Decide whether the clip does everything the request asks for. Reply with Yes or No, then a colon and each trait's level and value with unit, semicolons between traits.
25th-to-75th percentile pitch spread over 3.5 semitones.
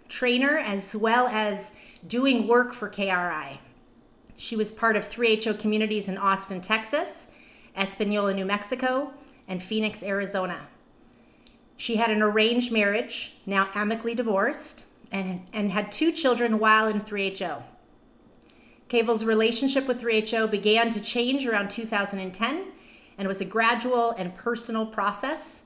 No: average, 3.0 semitones